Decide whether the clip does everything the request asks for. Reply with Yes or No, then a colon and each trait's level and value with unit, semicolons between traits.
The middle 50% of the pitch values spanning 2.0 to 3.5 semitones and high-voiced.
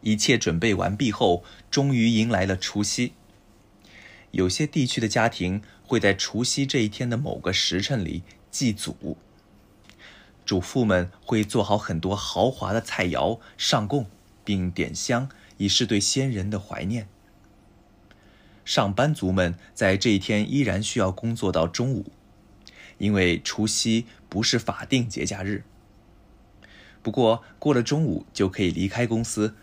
No: average, 2.7 semitones; low, 105 Hz